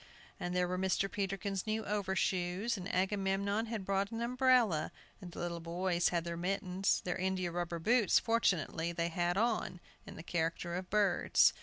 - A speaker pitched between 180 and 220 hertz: Yes, high, 190 Hz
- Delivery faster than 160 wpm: Yes, average, 170 wpm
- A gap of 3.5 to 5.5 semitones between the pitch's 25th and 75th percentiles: No, average, 2.7 semitones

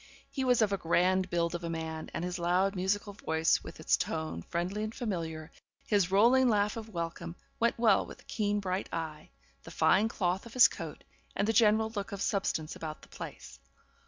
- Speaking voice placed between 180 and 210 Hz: Yes, high, 190 Hz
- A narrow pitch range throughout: No, average, 4.2 semitones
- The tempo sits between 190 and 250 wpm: Yes, average, 200 wpm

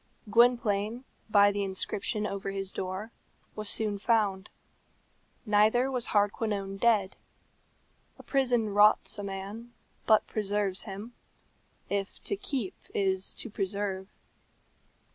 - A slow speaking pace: Yes, slow, 110 wpm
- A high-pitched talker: Yes, high, 205 Hz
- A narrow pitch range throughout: Yes, narrow, 2.2 semitones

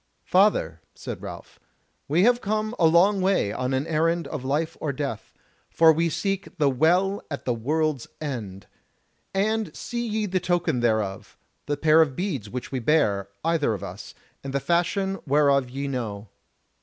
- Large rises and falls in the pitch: Yes, wide, 6.2 semitones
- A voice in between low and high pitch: Yes, medium, 155 Hz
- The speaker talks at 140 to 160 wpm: No, average, 170 wpm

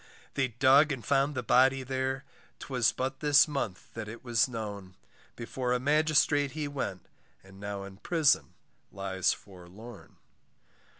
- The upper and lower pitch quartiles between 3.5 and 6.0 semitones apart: Yes, average, 5.2 semitones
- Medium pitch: No, low, 125 Hz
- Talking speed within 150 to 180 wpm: No, average, 140 wpm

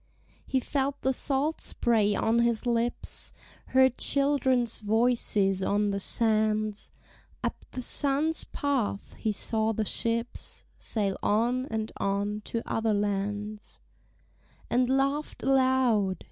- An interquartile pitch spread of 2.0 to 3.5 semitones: No, average, 3.9 semitones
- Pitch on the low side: No, high, 230 Hz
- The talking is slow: Yes, slow, 120 wpm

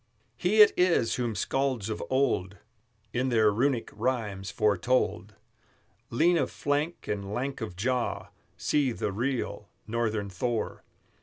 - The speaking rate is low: Yes, slow, 130 wpm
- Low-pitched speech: Yes, low, 115 Hz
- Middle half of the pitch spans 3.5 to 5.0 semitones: Yes, average, 4.5 semitones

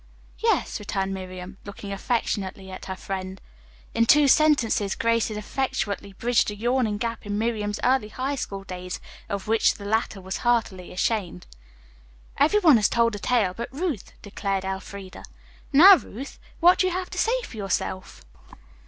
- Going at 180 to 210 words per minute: No, average, 160 wpm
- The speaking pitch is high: Yes, high, 210 Hz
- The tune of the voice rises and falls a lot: No, average, 4.1 semitones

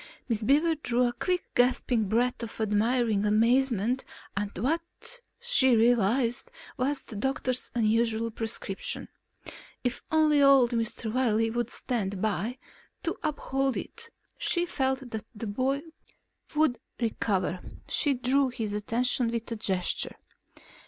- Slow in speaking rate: Yes, slow, 130 wpm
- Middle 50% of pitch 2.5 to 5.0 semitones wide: Yes, average, 3.4 semitones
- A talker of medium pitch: No, high, 240 Hz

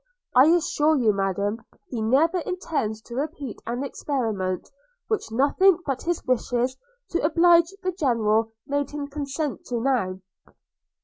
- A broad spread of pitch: Yes, wide, 5.7 semitones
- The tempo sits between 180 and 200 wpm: No, slow, 135 wpm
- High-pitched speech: Yes, very high, 270 Hz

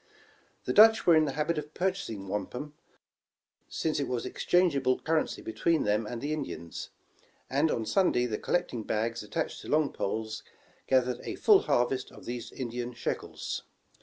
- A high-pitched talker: No, low, 130 Hz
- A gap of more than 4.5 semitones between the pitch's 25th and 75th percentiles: Yes, average, 5.3 semitones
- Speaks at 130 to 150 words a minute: No, average, 160 wpm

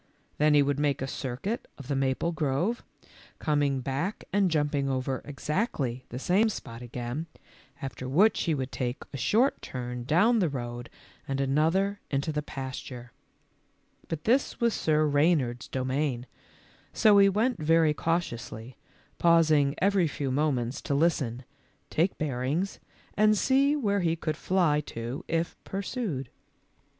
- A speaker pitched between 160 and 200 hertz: No, medium, 150 Hz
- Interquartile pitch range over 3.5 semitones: Yes, average, 5.2 semitones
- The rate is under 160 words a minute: Yes, average, 140 wpm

